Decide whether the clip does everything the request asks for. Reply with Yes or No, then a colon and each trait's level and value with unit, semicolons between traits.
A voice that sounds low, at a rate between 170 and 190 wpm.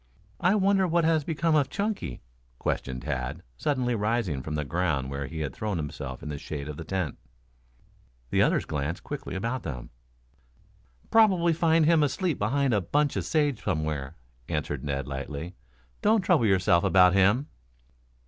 No: very low, 95 Hz; average, 160 wpm